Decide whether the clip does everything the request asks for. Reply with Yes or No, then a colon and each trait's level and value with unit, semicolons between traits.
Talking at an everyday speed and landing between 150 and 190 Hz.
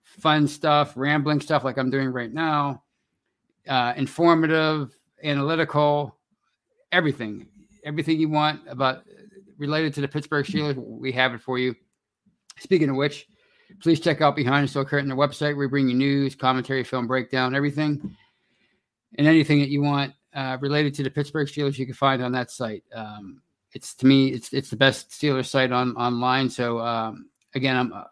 No: average, 175 wpm; medium, 140 Hz